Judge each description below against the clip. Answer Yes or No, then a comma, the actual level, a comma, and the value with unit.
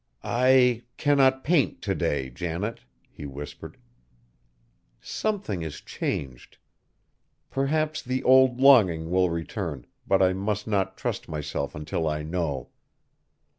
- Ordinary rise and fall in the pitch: No, wide, 8.9 semitones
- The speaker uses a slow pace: Yes, slow, 115 wpm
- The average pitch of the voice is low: Yes, very low, 95 Hz